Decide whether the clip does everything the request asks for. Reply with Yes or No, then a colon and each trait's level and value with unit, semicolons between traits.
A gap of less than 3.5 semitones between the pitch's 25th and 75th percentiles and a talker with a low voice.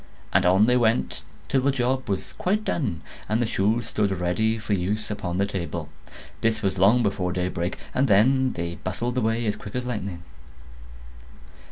No: average, 4.5 semitones; low, 105 Hz